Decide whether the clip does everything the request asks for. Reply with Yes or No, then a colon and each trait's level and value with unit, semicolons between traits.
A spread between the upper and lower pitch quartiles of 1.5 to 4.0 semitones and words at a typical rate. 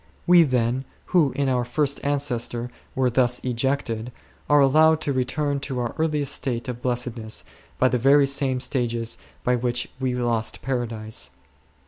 Yes: average, 2.7 semitones; average, 150 wpm